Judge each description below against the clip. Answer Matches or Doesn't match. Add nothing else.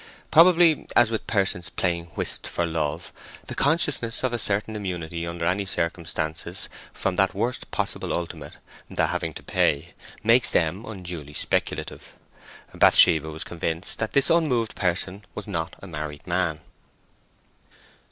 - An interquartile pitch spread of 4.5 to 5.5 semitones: Matches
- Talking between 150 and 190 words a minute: Doesn't match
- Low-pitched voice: Matches